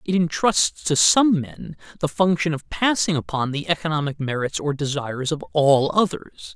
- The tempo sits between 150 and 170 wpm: Yes, average, 165 wpm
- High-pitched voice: No, medium, 155 Hz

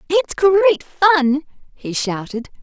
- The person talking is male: No, female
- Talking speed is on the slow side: Yes, slow, 115 wpm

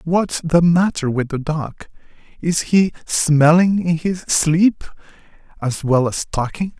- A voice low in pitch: No, medium, 160 Hz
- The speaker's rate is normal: No, slow, 130 wpm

